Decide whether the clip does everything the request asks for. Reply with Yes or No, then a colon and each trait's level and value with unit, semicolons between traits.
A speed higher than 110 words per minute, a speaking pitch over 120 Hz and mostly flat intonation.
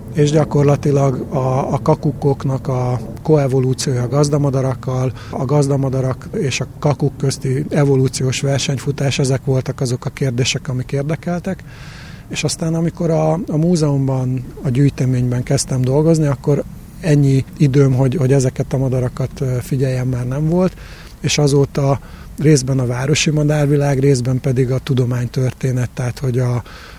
Yes: average, 130 wpm; low, 135 Hz; narrow, 2.2 semitones